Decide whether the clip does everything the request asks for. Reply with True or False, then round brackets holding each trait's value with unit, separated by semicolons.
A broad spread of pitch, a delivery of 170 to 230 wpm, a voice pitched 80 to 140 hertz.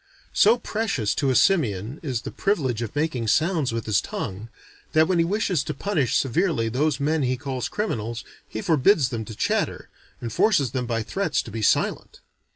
True (6.3 semitones; 185 wpm; 135 Hz)